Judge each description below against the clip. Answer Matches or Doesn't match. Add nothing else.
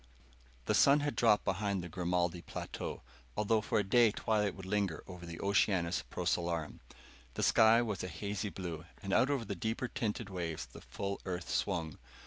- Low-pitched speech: Matches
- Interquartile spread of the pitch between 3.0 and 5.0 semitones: Matches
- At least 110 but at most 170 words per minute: Doesn't match